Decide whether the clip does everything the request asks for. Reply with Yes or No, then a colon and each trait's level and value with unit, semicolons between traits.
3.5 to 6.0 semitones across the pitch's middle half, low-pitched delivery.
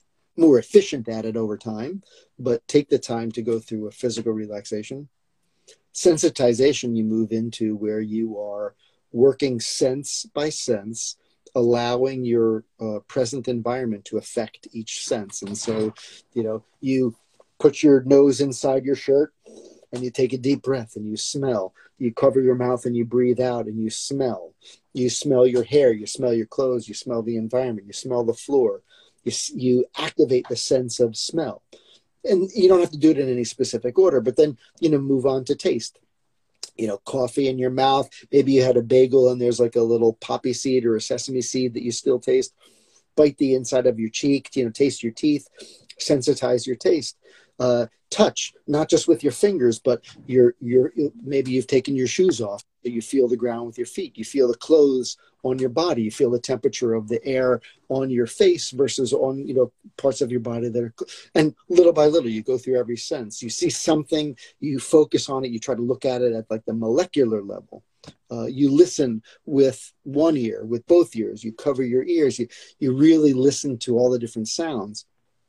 No: average, 3.1 semitones; low, 125 Hz